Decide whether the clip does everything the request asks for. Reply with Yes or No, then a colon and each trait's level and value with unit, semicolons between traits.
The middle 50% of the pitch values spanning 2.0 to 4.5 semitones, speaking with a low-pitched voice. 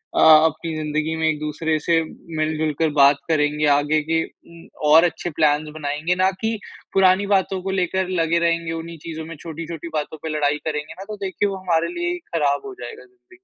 No: average, 2.9 semitones; medium, 160 Hz